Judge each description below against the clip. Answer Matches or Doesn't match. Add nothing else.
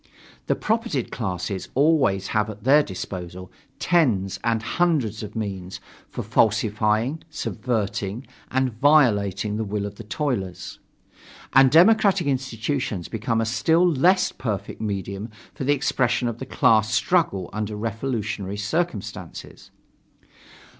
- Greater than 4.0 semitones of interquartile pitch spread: Matches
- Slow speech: Matches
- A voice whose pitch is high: Doesn't match